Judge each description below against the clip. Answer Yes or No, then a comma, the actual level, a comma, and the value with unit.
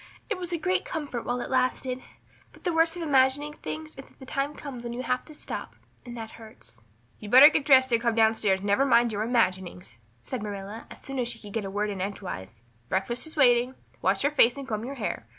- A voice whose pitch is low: No, high, 240 Hz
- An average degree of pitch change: Yes, average, 4.7 semitones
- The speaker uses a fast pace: Yes, fast, 240 wpm